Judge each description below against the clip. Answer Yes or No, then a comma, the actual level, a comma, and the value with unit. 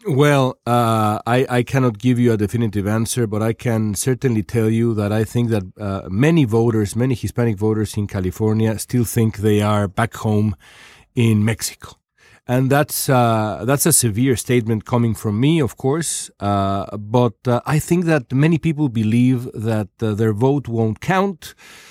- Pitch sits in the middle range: No, low, 115 Hz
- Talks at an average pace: Yes, average, 175 wpm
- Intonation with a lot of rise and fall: No, average, 3.3 semitones